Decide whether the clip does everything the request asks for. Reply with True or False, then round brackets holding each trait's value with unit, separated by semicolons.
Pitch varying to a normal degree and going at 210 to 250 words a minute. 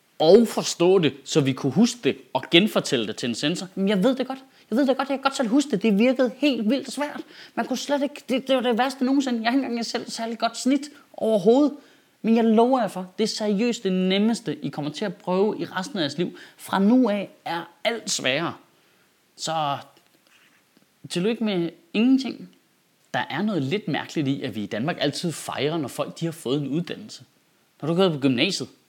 False (6.9 semitones; 220 wpm)